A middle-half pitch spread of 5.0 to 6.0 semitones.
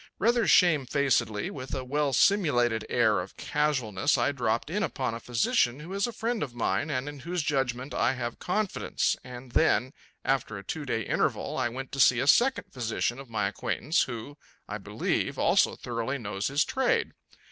No: average, 4.1 semitones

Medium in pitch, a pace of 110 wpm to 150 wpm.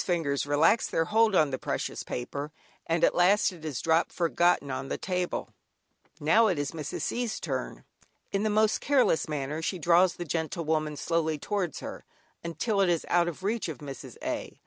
No: medium, 170 Hz; average, 185 wpm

